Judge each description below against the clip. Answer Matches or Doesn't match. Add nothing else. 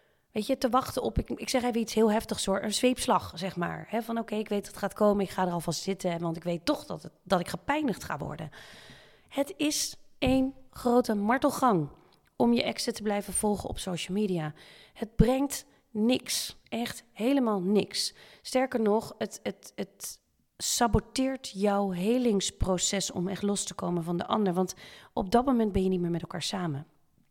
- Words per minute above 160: Matches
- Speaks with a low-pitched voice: Doesn't match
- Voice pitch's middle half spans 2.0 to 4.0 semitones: Doesn't match